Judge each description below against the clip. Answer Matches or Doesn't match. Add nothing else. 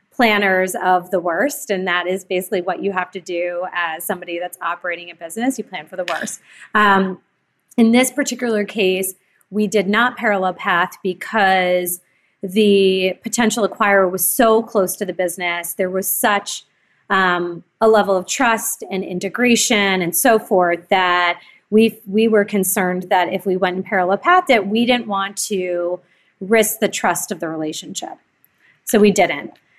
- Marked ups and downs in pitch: Doesn't match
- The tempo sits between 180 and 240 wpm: Doesn't match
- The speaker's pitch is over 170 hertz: Matches